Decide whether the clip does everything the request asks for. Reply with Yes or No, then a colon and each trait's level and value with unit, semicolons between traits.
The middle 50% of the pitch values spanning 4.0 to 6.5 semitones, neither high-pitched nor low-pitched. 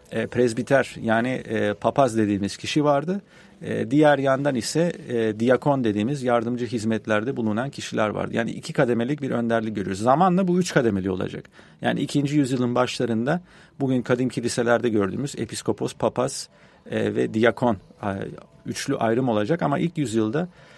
No: average, 4.3 semitones; low, 125 Hz